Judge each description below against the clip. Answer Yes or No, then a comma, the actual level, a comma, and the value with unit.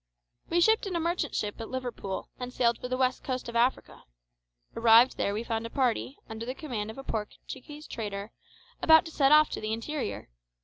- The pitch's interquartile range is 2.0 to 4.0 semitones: No, average, 4.7 semitones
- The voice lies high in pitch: Yes, very high, 250 Hz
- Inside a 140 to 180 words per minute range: No, fast, 205 wpm